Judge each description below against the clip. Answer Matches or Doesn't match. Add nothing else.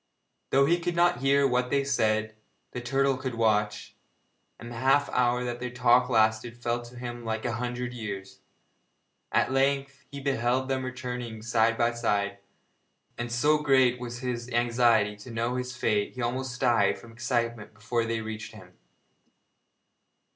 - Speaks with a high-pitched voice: Doesn't match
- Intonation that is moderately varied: Doesn't match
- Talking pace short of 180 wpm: Matches